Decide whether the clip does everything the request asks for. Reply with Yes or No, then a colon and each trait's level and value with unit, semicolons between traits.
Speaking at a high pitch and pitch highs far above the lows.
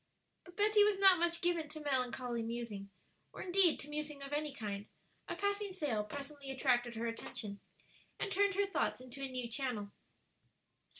Yes: very high, 280 Hz; wide, 6.8 semitones